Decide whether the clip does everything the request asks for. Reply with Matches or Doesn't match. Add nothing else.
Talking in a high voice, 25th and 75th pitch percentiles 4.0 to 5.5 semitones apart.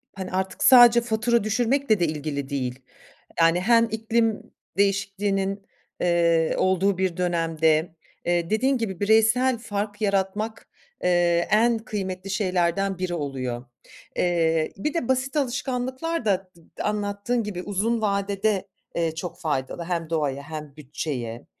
Matches